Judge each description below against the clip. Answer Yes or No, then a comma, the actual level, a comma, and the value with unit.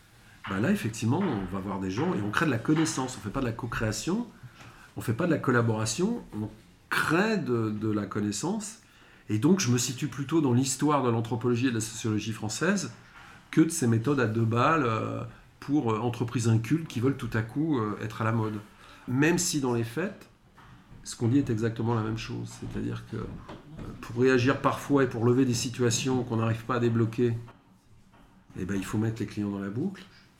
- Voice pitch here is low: Yes, low, 120 Hz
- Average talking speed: Yes, average, 210 wpm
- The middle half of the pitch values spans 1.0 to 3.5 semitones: No, average, 3.9 semitones